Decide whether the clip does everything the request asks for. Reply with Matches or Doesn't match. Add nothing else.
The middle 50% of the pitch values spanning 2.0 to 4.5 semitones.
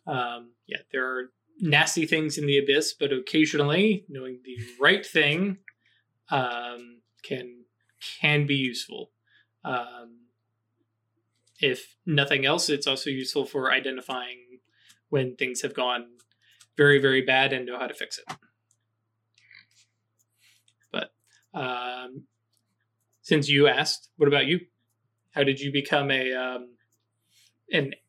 Matches